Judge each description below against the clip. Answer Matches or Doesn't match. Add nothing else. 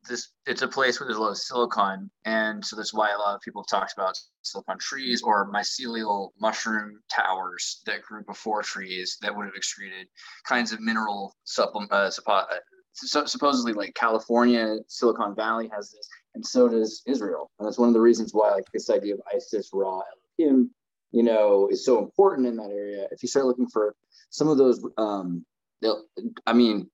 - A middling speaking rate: Matches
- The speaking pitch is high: Doesn't match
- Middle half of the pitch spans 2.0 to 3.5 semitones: Doesn't match